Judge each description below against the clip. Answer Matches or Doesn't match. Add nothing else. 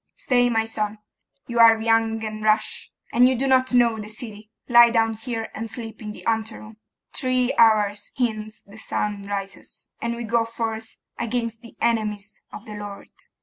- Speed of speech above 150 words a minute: Matches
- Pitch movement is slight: Matches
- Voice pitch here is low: Doesn't match